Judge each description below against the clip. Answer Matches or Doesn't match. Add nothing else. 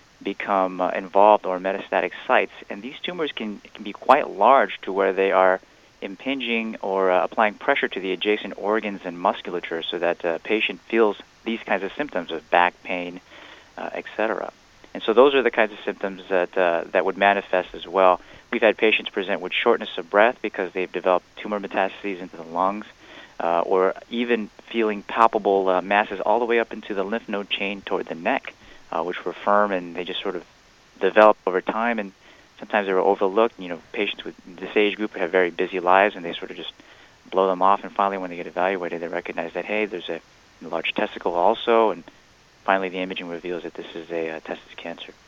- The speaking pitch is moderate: Doesn't match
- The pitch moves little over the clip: Matches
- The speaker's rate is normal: Doesn't match